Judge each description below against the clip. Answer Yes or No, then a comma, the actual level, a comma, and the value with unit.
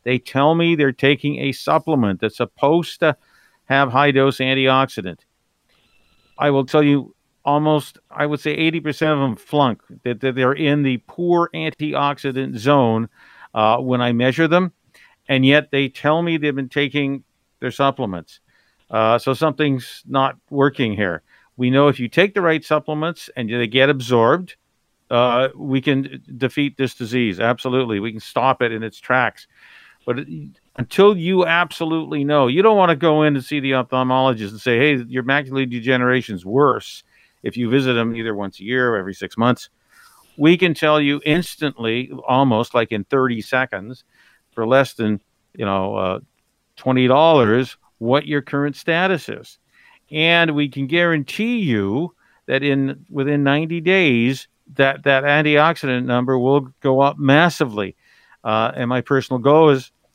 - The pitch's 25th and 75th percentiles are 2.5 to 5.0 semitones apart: Yes, average, 3.3 semitones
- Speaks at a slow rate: No, average, 160 wpm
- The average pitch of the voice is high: No, low, 135 Hz